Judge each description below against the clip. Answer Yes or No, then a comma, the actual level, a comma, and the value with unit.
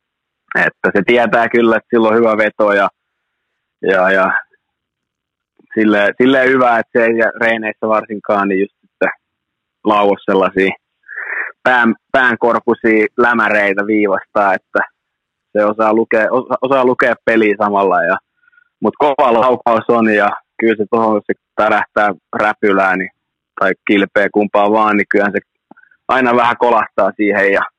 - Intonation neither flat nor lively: No, narrow, 2.1 semitones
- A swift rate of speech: No, average, 125 wpm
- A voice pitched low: Yes, low, 110 Hz